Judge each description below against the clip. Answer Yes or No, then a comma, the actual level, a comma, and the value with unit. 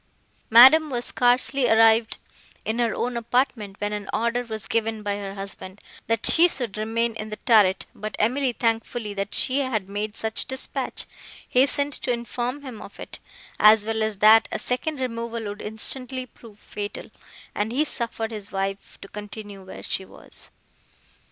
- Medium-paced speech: Yes, average, 165 wpm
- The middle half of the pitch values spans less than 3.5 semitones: Yes, average, 2.8 semitones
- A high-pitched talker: Yes, high, 225 Hz